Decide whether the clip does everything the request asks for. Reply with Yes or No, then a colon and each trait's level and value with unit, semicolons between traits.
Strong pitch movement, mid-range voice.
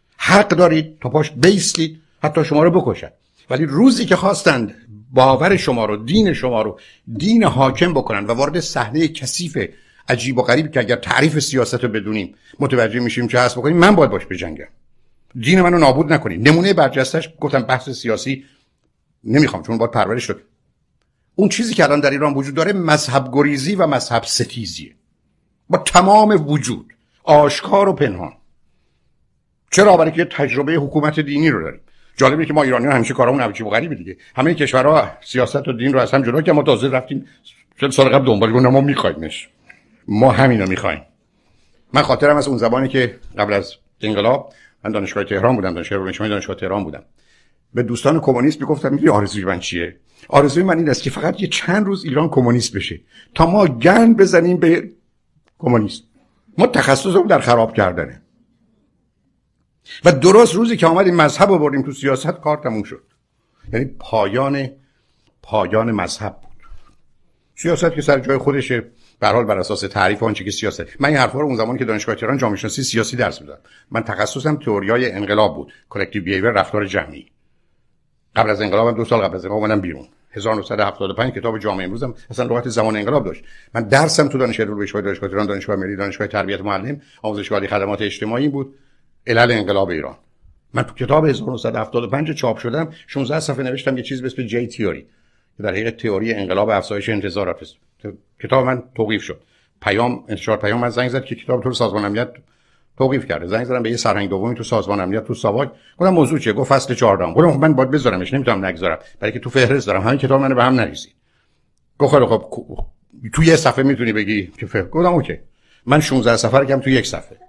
No: wide, 5.7 semitones; low, 130 Hz